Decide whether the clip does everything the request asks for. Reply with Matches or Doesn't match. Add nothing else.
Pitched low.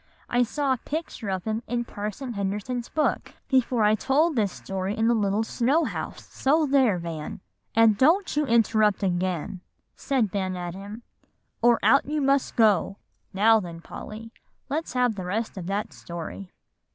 Doesn't match